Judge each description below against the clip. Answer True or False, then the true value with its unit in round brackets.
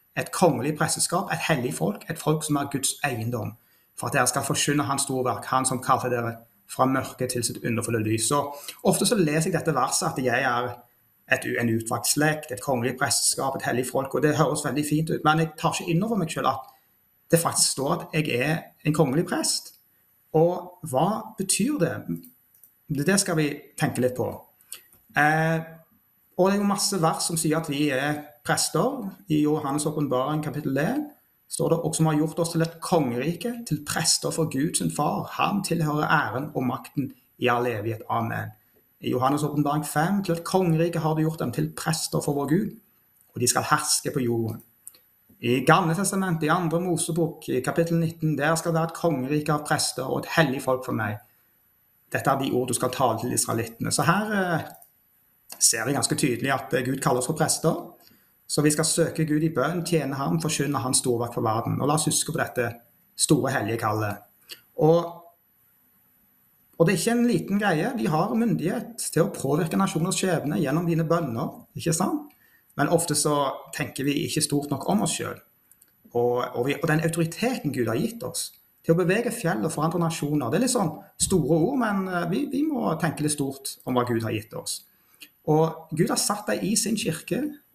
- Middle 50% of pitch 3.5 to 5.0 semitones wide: True (3.9 semitones)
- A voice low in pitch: False (155 Hz)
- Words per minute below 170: False (195 wpm)